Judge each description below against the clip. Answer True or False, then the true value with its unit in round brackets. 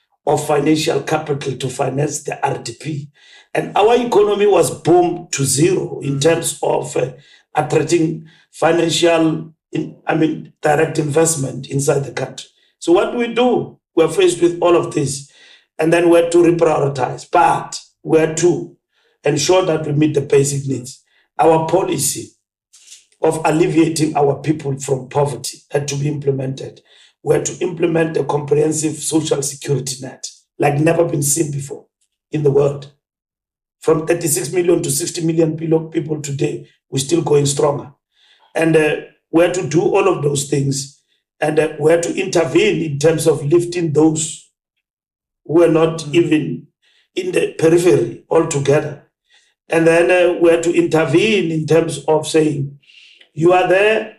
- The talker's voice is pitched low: False (160 Hz)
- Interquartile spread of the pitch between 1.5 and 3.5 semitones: True (2.7 semitones)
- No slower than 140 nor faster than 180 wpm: True (150 wpm)